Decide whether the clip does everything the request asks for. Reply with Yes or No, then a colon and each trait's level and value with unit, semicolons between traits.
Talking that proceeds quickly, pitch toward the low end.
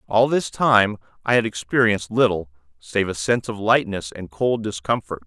No: average, 170 wpm; low, 105 Hz